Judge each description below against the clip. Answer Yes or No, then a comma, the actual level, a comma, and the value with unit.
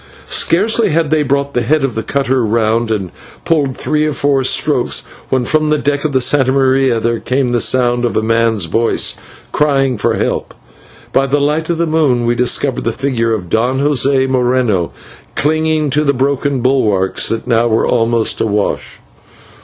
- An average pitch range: Yes, average, 3.6 semitones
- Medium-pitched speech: No, low, 130 Hz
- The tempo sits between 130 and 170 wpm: No, average, 185 wpm